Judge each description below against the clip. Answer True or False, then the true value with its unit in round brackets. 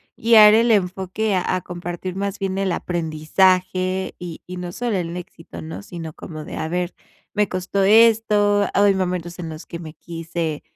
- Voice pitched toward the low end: False (185 Hz)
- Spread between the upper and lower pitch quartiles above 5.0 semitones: False (2.8 semitones)